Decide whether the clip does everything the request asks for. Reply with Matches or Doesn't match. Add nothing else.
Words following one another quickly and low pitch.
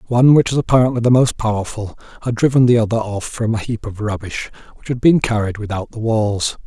Matches